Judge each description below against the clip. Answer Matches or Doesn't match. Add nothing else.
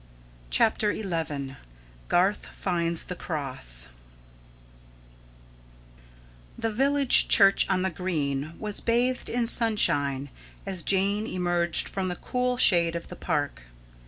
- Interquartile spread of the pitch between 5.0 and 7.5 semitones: Matches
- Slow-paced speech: Matches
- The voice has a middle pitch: Matches